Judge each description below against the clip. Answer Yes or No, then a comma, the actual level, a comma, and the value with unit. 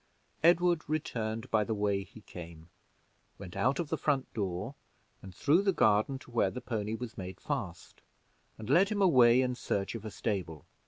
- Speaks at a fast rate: No, average, 180 wpm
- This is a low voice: Yes, low, 115 Hz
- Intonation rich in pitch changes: Yes, wide, 5.8 semitones